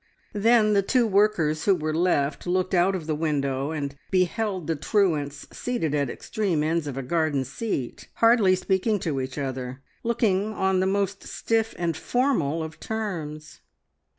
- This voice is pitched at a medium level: Yes, medium, 175 Hz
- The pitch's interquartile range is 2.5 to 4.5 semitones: No, wide, 5.5 semitones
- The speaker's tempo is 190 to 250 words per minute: No, average, 160 wpm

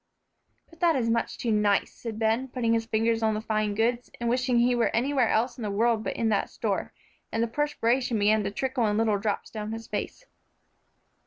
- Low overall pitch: No, high, 230 Hz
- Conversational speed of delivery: No, fast, 215 wpm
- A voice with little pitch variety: Yes, narrow, 2.2 semitones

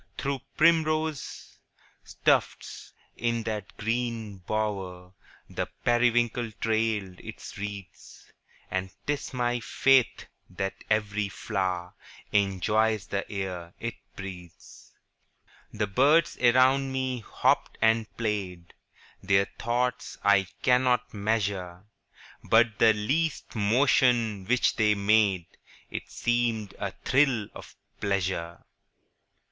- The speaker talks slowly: Yes, slow, 100 wpm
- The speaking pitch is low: Yes, low, 110 Hz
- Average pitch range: Yes, average, 3.9 semitones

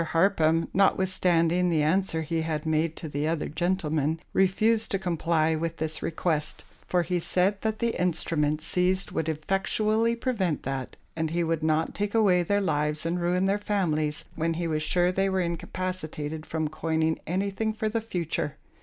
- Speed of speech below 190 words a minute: Yes, average, 170 wpm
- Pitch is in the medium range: Yes, medium, 170 Hz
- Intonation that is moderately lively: Yes, average, 3.3 semitones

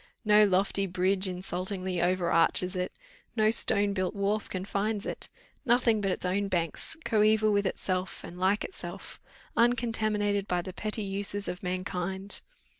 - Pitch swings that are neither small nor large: No, narrow, 2.3 semitones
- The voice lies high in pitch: Yes, high, 195 Hz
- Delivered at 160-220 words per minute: No, average, 145 wpm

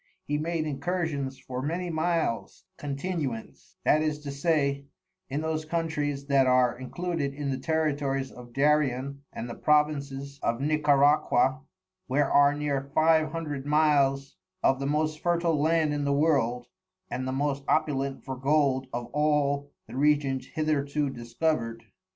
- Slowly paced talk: No, average, 145 wpm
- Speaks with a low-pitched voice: No, medium, 145 Hz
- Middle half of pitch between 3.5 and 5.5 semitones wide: No, narrow, 2.4 semitones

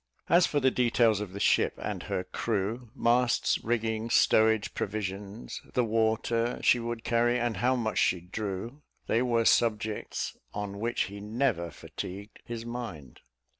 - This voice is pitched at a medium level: No, low, 115 Hz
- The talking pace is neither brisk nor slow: Yes, average, 150 wpm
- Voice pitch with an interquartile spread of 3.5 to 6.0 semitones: No, narrow, 2.6 semitones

